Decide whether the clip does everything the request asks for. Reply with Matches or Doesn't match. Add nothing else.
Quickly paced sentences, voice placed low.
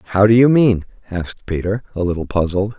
Doesn't match